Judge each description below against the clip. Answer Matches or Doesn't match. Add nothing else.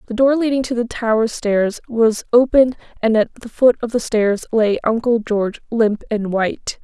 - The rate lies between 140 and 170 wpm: Doesn't match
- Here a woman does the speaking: Matches